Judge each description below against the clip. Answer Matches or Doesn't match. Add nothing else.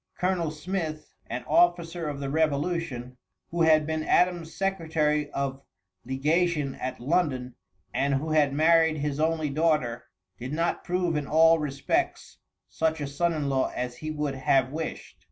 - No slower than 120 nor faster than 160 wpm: Matches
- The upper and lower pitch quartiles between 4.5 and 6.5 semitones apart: Doesn't match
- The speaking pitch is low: Doesn't match